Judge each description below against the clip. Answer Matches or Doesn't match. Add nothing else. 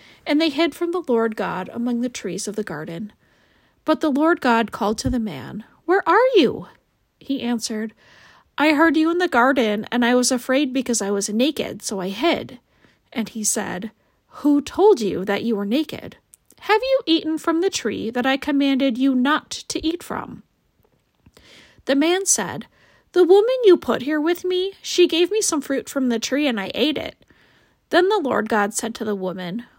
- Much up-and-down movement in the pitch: Matches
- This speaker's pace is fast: Doesn't match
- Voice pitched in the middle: Doesn't match